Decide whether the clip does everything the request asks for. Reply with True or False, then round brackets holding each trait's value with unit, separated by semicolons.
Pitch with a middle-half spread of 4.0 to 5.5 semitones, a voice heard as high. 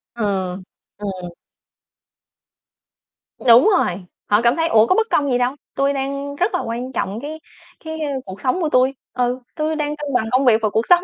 True (4.3 semitones; 260 Hz)